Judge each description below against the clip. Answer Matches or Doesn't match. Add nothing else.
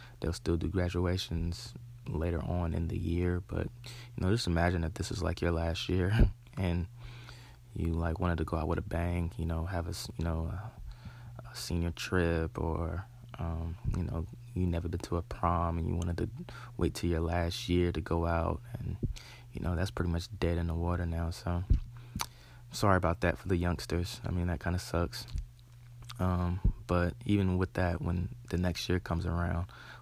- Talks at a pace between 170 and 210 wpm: Matches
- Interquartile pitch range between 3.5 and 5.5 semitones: Matches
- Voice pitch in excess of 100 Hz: Doesn't match